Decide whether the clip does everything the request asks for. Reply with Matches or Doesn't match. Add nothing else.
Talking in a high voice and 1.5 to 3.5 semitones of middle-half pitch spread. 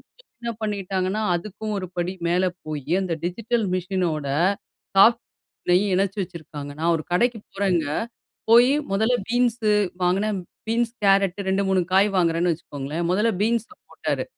Doesn't match